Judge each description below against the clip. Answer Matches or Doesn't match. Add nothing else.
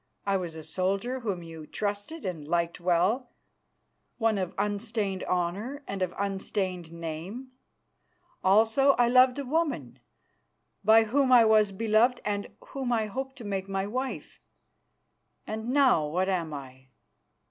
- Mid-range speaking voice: Doesn't match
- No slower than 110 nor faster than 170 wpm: Matches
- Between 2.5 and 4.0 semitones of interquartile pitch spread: Doesn't match